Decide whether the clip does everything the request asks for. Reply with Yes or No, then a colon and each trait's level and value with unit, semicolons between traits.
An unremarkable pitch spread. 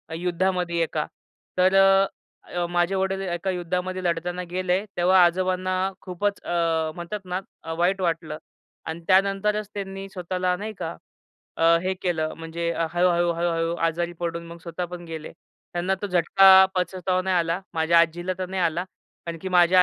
No: narrow, 1.7 semitones